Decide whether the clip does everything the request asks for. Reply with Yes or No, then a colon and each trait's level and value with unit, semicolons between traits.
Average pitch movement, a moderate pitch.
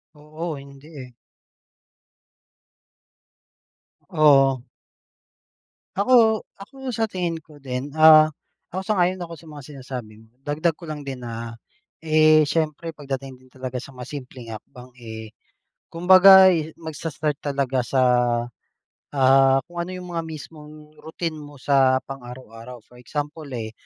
Yes: average, 4.0 semitones; medium, 145 Hz